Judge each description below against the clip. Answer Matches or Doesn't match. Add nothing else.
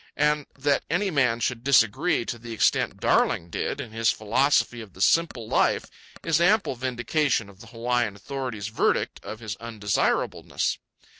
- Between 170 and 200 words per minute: Doesn't match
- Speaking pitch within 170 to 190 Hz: Doesn't match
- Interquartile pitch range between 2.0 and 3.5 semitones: Doesn't match